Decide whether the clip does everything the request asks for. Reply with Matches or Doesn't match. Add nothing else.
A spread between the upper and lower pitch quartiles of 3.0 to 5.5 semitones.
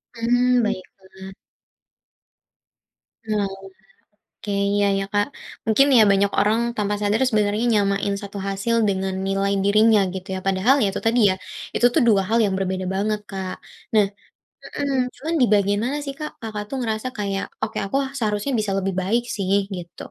Doesn't match